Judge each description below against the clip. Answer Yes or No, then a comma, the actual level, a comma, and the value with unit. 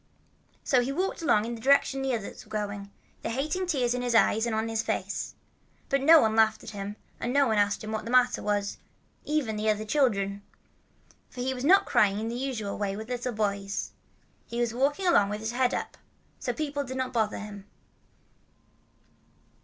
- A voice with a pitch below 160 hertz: No, high, 230 Hz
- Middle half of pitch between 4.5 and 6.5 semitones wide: No, average, 3.8 semitones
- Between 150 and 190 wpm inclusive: No, average, 200 wpm